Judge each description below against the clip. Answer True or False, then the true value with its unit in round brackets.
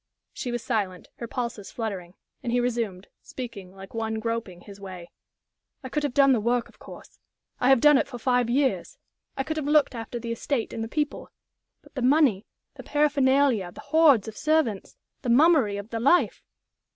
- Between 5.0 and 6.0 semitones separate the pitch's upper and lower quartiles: False (4.2 semitones)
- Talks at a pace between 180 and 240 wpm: True (190 wpm)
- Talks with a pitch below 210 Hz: False (240 Hz)